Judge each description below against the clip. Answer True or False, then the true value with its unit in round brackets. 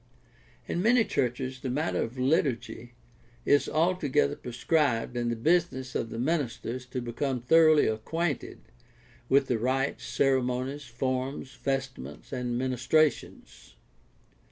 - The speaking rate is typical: False (125 wpm)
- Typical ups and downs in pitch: True (3.2 semitones)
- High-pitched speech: False (130 Hz)